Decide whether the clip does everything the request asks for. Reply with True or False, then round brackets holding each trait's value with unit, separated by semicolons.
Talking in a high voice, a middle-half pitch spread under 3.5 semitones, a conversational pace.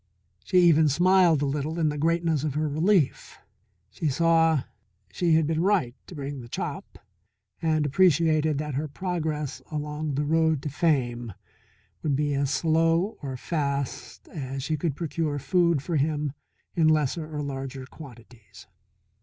False (150 Hz; 2.7 semitones; 150 wpm)